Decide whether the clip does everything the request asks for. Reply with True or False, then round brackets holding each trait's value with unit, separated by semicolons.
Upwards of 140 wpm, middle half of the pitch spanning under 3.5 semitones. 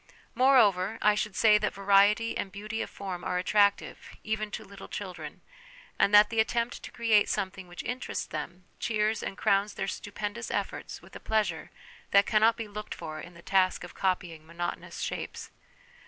True (180 wpm; 2.7 semitones)